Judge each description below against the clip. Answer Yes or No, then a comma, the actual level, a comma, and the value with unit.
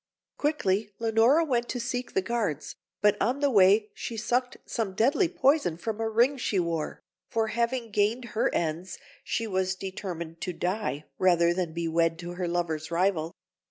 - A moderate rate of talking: Yes, average, 170 wpm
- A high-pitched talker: Yes, high, 205 Hz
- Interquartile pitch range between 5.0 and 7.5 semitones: Yes, average, 5.3 semitones